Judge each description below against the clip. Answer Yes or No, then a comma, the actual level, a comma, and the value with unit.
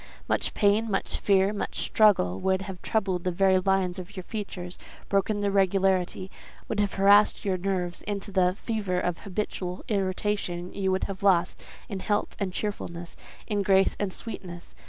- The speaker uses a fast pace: No, average, 165 wpm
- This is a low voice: No, high, 195 Hz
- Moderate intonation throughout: No, narrow, 1.9 semitones